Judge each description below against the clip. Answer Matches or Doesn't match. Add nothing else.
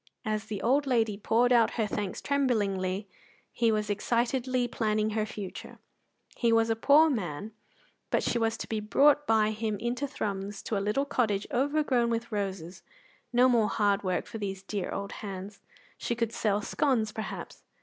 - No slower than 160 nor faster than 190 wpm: Matches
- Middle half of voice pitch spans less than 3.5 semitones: Matches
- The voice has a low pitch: Doesn't match